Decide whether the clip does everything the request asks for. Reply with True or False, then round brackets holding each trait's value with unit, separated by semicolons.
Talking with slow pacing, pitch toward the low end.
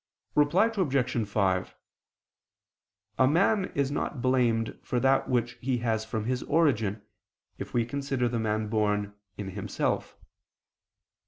True (130 wpm; 120 Hz)